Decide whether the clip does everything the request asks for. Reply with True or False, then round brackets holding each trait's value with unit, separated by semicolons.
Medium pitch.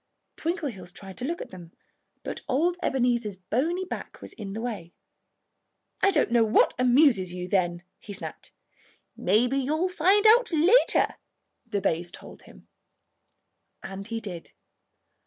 False (235 Hz)